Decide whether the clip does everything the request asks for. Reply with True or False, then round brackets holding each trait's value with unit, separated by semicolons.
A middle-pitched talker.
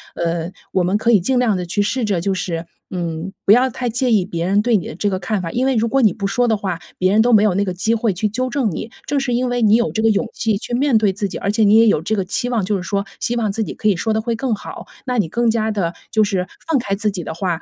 False (210 Hz)